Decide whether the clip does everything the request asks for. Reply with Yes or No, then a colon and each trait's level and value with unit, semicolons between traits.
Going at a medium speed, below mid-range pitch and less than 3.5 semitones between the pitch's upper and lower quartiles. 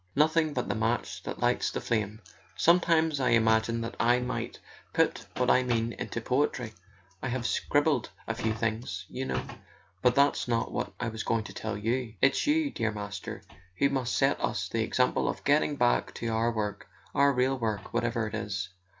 Yes: average, 190 wpm; low, 120 Hz; average, 3.1 semitones